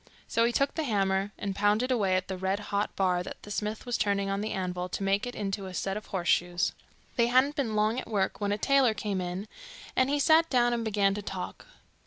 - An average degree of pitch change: Yes, average, 3.5 semitones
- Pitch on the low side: No, high, 205 Hz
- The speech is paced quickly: Yes, fast, 240 wpm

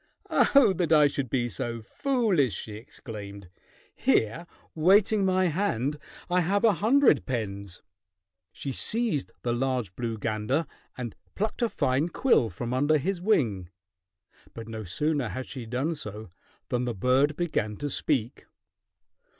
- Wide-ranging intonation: Yes, wide, 7.7 semitones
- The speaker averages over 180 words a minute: No, average, 140 wpm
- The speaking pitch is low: Yes, low, 130 Hz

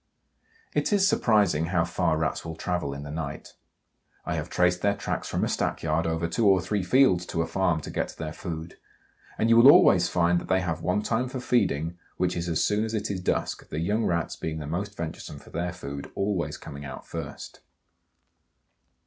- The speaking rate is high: Yes, fast, 210 wpm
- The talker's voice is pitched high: No, very low, 90 Hz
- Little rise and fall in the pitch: No, average, 3.8 semitones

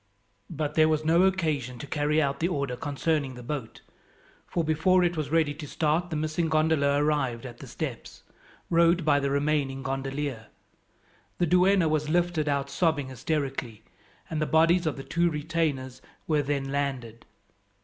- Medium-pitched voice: Yes, medium, 150 Hz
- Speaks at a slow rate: No, average, 165 wpm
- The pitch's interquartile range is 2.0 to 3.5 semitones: Yes, average, 2.8 semitones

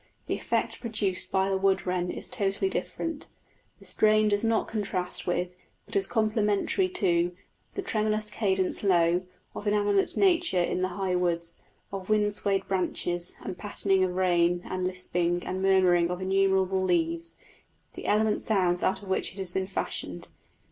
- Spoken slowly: No, average, 160 wpm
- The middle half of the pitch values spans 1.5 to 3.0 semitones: Yes, narrow, 2.6 semitones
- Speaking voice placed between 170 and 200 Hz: Yes, high, 190 Hz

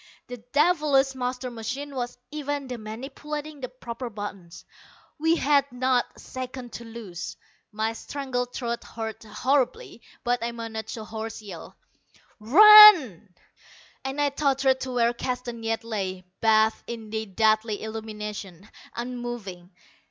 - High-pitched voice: Yes, high, 240 Hz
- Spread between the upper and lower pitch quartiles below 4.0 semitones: Yes, average, 3.4 semitones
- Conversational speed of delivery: No, slow, 130 wpm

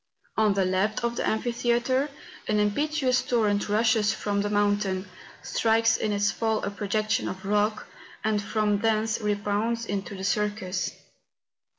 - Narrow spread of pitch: Yes, narrow, 1.8 semitones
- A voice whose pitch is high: Yes, high, 210 Hz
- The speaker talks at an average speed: Yes, average, 150 wpm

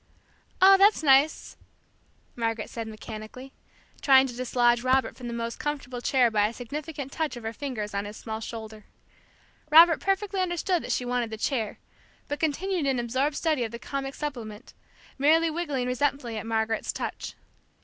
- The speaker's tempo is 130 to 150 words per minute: No, average, 165 wpm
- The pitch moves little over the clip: No, average, 4.5 semitones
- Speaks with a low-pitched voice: No, very high, 255 Hz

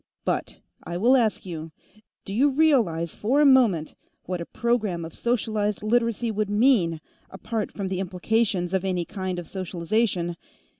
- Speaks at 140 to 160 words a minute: Yes, average, 155 wpm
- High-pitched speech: Yes, high, 200 Hz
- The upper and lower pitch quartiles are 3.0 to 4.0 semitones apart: No, average, 4.8 semitones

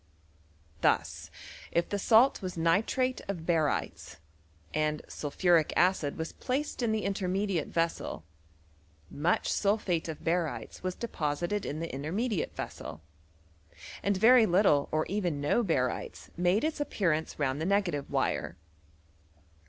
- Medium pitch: Yes, medium, 175 Hz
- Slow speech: Yes, slow, 130 wpm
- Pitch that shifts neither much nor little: Yes, average, 4.8 semitones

